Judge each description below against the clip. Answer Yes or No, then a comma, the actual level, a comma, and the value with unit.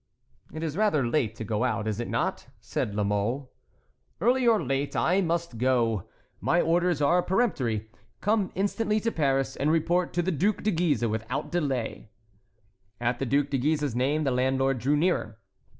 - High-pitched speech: No, medium, 140 Hz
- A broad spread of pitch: Yes, wide, 6.5 semitones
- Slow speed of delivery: No, average, 170 wpm